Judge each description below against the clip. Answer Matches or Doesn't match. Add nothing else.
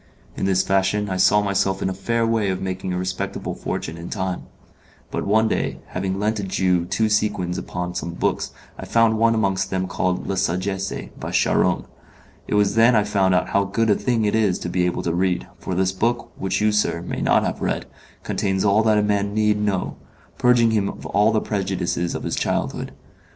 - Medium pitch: Doesn't match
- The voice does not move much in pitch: Matches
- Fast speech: Matches